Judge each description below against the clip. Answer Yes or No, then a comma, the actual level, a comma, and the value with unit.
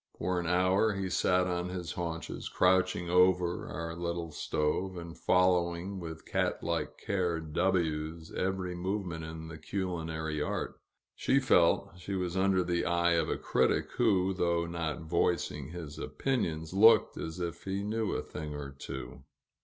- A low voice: Yes, very low, 85 Hz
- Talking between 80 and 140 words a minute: No, average, 160 wpm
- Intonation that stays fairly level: Yes, narrow, 2.2 semitones